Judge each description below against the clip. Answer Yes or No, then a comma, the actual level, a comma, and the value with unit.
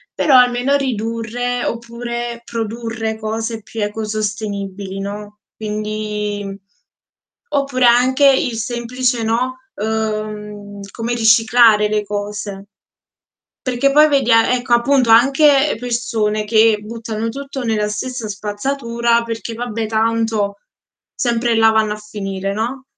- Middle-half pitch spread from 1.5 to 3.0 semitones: Yes, narrow, 2.4 semitones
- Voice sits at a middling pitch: No, high, 225 Hz